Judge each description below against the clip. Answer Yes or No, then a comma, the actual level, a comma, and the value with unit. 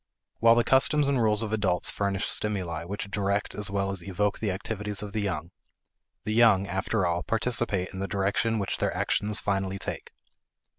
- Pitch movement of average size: No, narrow, 2.0 semitones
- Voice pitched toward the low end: Yes, low, 100 Hz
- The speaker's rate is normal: Yes, average, 185 wpm